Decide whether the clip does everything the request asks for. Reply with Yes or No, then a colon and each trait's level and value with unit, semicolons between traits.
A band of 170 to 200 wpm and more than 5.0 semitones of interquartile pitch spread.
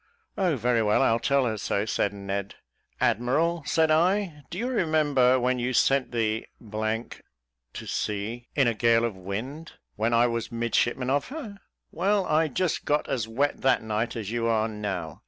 Yes: average, 175 wpm; wide, 5.4 semitones